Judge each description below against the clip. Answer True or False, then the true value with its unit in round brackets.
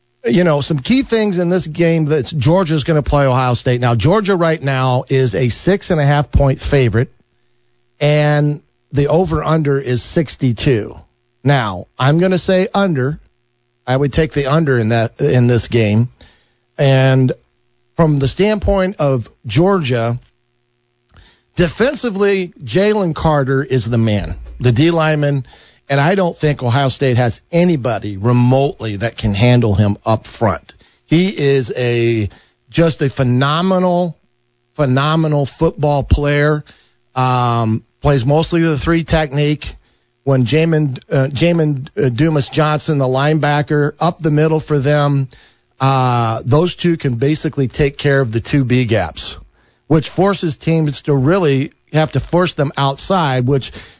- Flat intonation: False (4.6 semitones)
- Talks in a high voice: False (140 Hz)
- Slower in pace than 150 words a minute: True (140 wpm)